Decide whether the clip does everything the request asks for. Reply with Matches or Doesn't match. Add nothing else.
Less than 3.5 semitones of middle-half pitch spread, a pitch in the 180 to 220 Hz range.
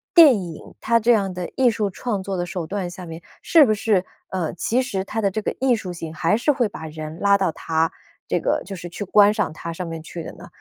Doesn't match